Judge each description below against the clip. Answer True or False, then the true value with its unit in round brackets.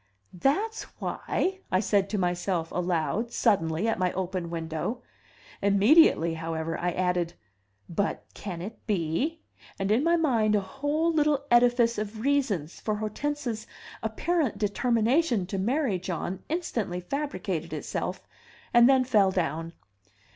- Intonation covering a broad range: True (6.6 semitones)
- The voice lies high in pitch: True (210 Hz)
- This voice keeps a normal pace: False (130 wpm)